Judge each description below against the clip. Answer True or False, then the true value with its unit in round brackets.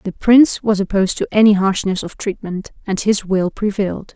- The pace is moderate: True (190 wpm)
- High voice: True (200 Hz)